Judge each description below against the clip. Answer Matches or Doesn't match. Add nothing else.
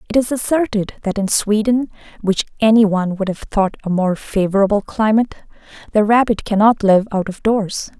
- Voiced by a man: Doesn't match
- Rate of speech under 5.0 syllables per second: Doesn't match